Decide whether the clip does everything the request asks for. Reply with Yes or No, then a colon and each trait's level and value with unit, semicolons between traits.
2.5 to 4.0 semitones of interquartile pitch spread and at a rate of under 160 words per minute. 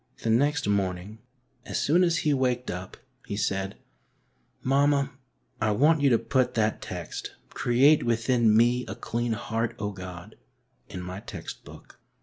No: average, 4.7 semitones; average, 150 wpm